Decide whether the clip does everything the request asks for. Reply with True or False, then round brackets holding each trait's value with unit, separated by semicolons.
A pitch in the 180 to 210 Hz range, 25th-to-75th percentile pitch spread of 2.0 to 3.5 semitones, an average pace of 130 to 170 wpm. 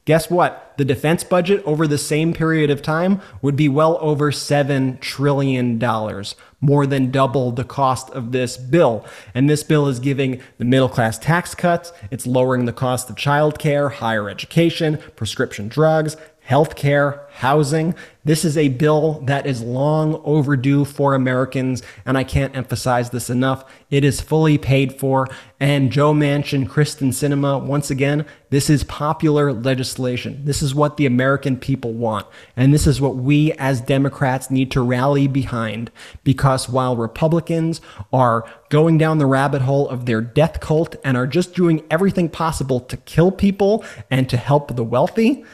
False (140 Hz; 2.9 semitones; 165 wpm)